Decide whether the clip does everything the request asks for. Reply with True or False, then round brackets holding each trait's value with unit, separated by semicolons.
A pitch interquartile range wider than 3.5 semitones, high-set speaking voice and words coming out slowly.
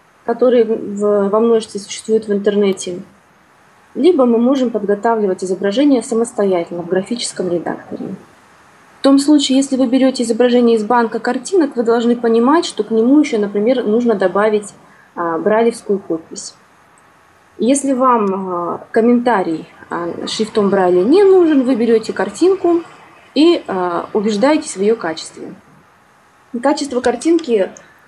False (4.5 semitones; 230 Hz; 125 wpm)